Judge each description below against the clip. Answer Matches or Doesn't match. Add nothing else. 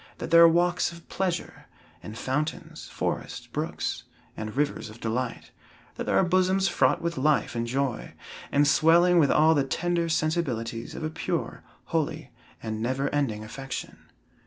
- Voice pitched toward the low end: Doesn't match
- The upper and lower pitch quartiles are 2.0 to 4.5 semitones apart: Doesn't match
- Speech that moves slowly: Doesn't match